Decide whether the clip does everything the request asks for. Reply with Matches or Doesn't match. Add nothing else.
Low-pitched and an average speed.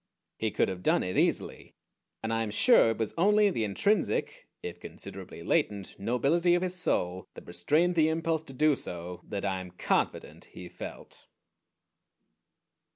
Matches